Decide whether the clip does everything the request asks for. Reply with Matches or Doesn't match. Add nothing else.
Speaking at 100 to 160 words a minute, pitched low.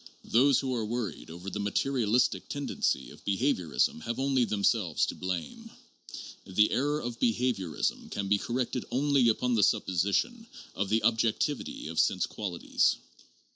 Matches